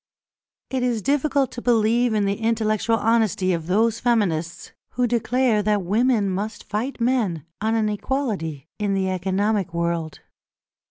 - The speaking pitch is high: Yes, high, 215 Hz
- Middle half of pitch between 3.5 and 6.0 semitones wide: Yes, average, 3.9 semitones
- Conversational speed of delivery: Yes, average, 145 wpm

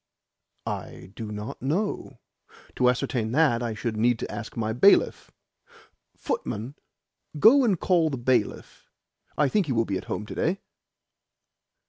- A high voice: No, low, 125 Hz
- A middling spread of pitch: No, wide, 6.3 semitones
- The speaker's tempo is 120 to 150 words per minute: Yes, average, 145 wpm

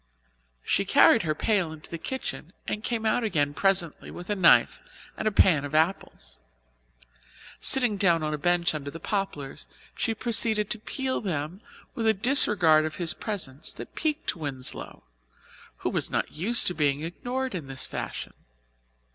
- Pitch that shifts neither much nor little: No, wide, 5.9 semitones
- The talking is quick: No, average, 165 wpm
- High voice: No, medium, 175 Hz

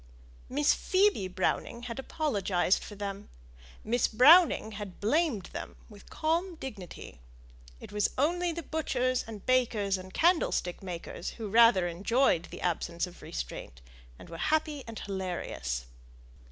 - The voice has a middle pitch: No, high, 220 Hz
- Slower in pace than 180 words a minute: Yes, slow, 135 wpm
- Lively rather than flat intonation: Yes, wide, 7.5 semitones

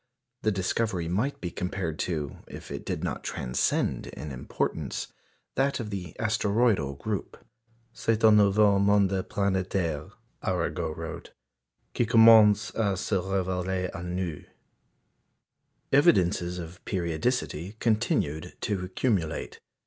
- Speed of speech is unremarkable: No, slow, 115 wpm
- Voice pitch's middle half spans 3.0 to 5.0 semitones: Yes, average, 3.6 semitones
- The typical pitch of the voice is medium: No, very low, 95 Hz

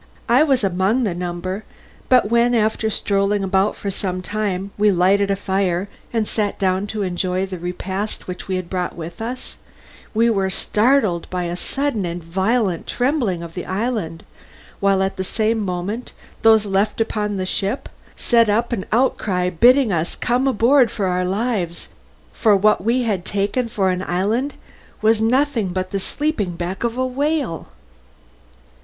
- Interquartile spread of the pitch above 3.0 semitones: Yes, average, 3.9 semitones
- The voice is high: Yes, high, 200 Hz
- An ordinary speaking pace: Yes, average, 170 wpm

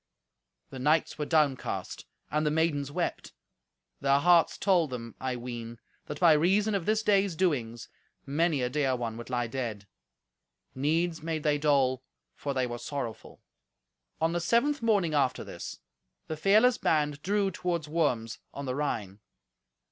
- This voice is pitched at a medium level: Yes, medium, 150 Hz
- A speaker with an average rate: Yes, average, 155 wpm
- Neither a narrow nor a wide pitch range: Yes, average, 5.0 semitones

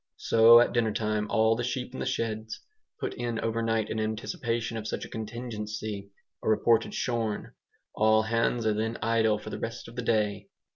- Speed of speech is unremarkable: Yes, average, 185 wpm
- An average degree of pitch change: No, narrow, 1.2 semitones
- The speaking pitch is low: Yes, low, 110 Hz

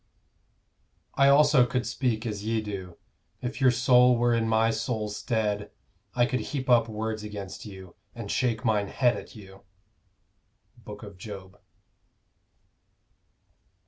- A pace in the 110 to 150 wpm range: Yes, slow, 135 wpm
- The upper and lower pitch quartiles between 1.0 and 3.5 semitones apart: Yes, average, 2.9 semitones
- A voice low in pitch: Yes, low, 110 Hz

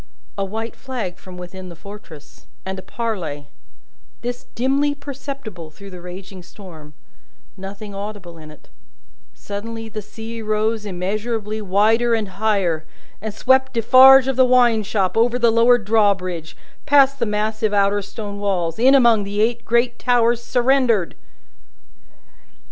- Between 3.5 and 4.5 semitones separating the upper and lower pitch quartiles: Yes, average, 3.8 semitones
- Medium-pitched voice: No, high, 215 Hz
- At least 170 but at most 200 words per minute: No, average, 140 wpm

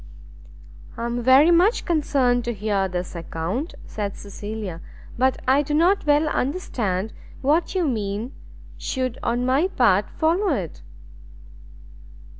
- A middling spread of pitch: No, wide, 6.5 semitones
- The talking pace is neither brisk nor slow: No, slow, 125 wpm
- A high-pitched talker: Yes, very high, 250 Hz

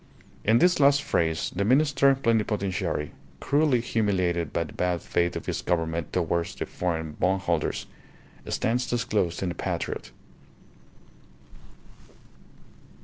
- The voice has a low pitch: Yes, very low, 95 Hz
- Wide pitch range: Yes, wide, 6.2 semitones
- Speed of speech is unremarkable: No, slow, 115 wpm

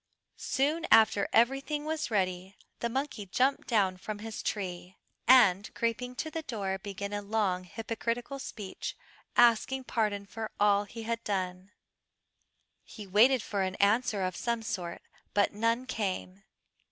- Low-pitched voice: No, high, 215 Hz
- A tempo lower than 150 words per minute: Yes, average, 140 wpm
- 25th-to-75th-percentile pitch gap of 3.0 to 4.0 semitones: Yes, average, 3.5 semitones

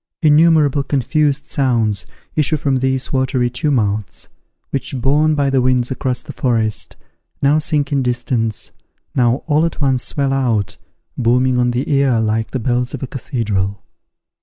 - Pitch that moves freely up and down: No, average, 2.8 semitones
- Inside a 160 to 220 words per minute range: No, average, 150 wpm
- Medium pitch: No, low, 130 Hz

